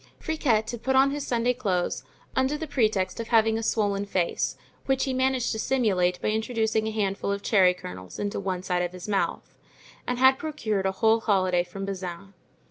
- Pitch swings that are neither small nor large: Yes, average, 4.6 semitones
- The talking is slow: No, average, 200 wpm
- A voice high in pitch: Yes, high, 215 Hz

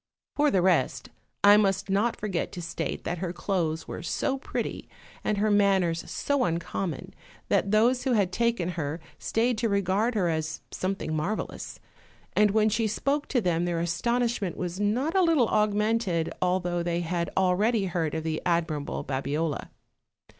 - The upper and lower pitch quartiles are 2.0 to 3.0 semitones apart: No, average, 4.3 semitones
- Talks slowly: No, average, 160 wpm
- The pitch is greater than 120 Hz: Yes, high, 190 Hz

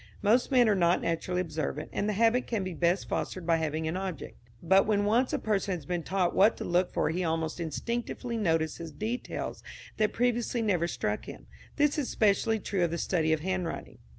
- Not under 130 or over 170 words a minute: No, fast, 205 wpm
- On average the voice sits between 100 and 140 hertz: No, medium, 185 Hz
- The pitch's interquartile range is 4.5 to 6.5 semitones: Yes, average, 4.8 semitones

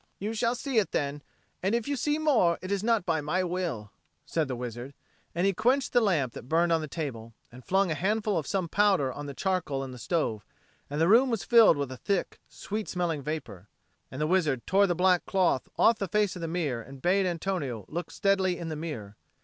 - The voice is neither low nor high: Yes, medium, 175 Hz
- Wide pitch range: Yes, wide, 5.8 semitones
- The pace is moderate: No, fast, 230 wpm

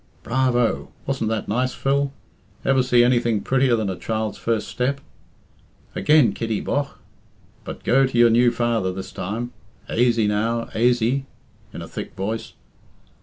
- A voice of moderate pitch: No, low, 120 Hz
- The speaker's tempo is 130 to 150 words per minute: Yes, average, 145 wpm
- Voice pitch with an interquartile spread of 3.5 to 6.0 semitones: No, narrow, 2.5 semitones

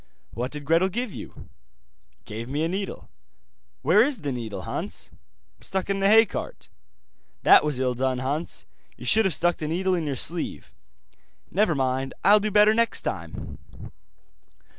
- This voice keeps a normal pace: Yes, average, 160 wpm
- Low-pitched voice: No, medium, 170 Hz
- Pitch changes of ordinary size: No, wide, 6.9 semitones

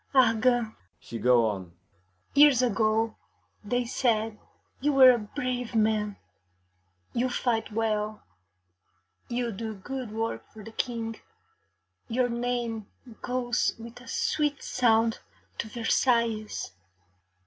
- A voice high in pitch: Yes, high, 230 Hz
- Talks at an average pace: No, slow, 110 wpm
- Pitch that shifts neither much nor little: No, narrow, 2.3 semitones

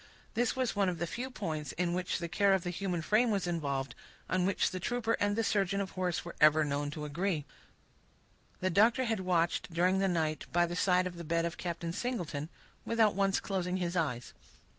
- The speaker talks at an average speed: No, fast, 210 wpm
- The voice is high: No, medium, 180 Hz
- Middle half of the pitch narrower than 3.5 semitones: Yes, average, 3.0 semitones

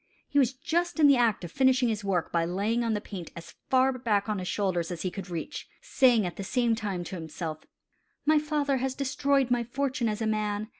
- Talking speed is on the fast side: Yes, fast, 230 wpm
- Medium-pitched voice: No, high, 225 Hz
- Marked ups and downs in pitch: Yes, wide, 5.7 semitones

